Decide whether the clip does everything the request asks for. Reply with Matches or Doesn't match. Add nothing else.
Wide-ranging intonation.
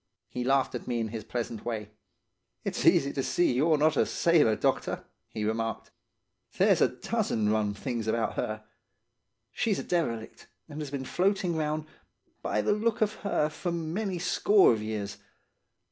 Matches